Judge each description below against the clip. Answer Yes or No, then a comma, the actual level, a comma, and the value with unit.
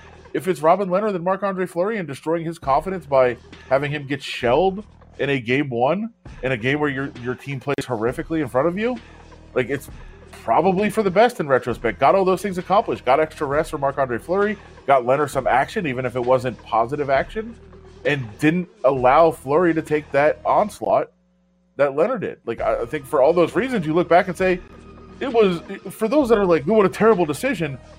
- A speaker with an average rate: No, fast, 210 wpm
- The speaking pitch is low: No, medium, 155 Hz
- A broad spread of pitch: Yes, wide, 6.2 semitones